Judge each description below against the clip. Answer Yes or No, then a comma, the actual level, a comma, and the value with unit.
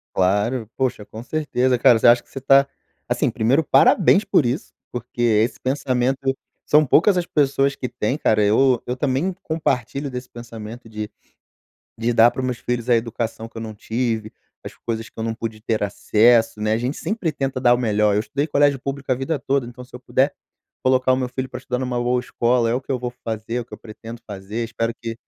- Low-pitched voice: Yes, low, 125 Hz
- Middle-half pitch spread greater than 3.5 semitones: No, average, 2.8 semitones